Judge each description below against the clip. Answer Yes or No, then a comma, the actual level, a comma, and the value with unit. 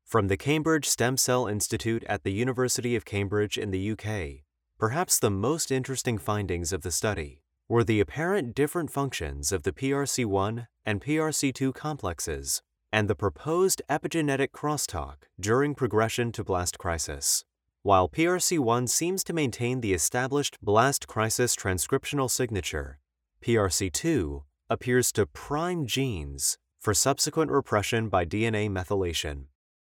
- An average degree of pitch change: No, wide, 6.1 semitones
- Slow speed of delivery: Yes, slow, 130 wpm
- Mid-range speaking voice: No, low, 115 Hz